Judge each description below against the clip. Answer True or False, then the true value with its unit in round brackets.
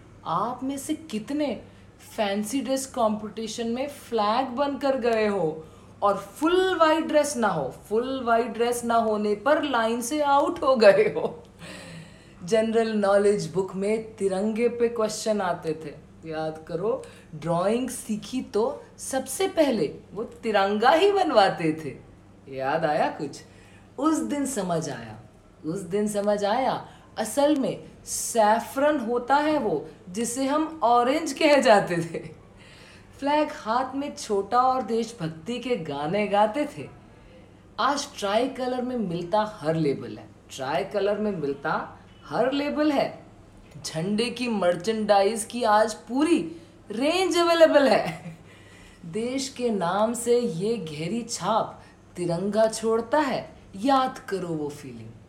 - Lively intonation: True (6.9 semitones)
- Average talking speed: True (130 wpm)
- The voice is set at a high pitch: True (220 Hz)